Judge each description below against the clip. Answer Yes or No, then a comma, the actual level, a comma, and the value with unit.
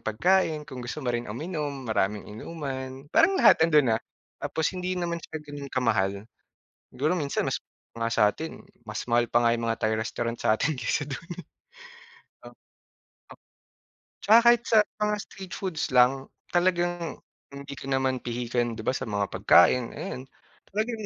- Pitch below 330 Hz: Yes, low, 135 Hz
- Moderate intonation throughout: No, wide, 6.1 semitones